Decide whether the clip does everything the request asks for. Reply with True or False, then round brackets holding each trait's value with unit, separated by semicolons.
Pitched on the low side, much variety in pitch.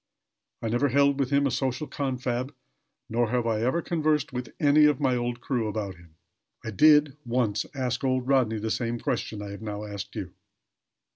False (125 Hz; 3.8 semitones)